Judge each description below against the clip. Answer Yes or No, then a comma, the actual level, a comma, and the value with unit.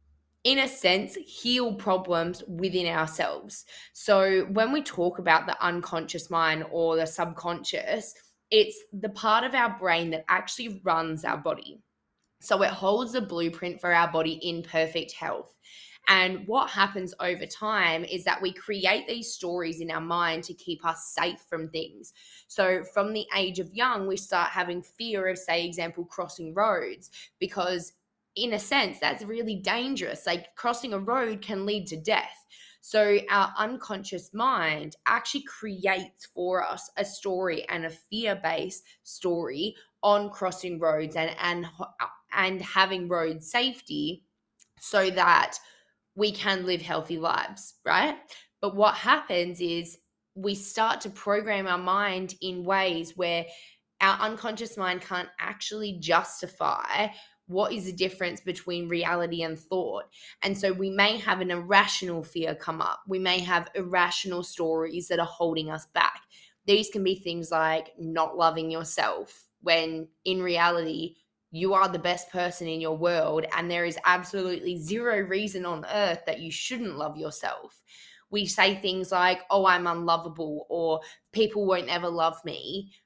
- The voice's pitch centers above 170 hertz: Yes, medium, 185 Hz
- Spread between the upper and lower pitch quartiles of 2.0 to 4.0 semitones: Yes, average, 3.3 semitones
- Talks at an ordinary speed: Yes, average, 155 wpm